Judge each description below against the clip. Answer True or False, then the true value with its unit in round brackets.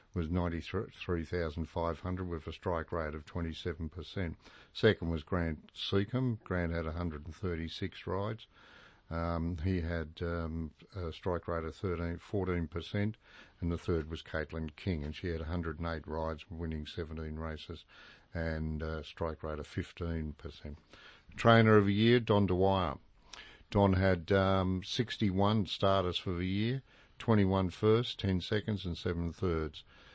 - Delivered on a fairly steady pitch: False (3.0 semitones)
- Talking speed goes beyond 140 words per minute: False (135 wpm)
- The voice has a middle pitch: False (85 Hz)